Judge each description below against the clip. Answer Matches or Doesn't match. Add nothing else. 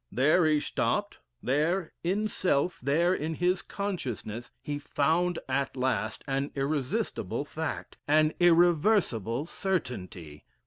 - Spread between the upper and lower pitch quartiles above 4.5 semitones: Matches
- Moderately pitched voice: Matches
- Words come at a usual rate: Doesn't match